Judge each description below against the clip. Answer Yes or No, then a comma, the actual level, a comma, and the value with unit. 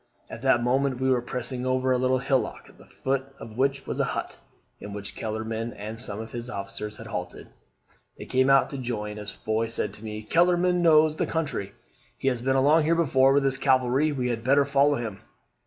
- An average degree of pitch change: Yes, average, 3.5 semitones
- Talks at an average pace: No, fast, 215 wpm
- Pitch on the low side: Yes, low, 130 Hz